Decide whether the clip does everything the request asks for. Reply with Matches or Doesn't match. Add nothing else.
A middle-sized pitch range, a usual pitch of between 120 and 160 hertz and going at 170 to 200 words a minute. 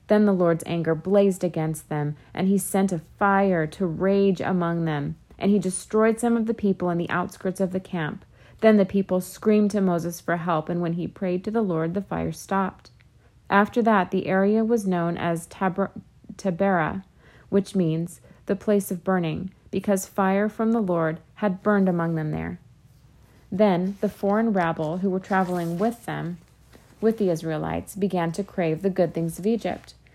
Doesn't match